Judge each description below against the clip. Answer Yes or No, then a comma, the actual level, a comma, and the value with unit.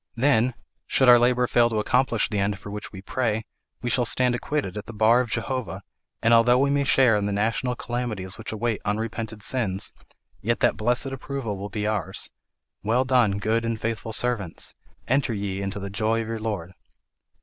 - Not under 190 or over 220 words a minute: Yes, average, 195 wpm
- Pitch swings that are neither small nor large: Yes, average, 3.0 semitones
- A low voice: Yes, low, 115 Hz